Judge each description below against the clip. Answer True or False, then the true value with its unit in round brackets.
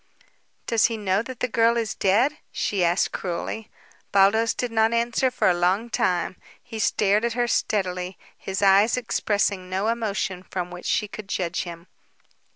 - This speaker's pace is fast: False (165 wpm)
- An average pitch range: True (3.6 semitones)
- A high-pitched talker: True (205 Hz)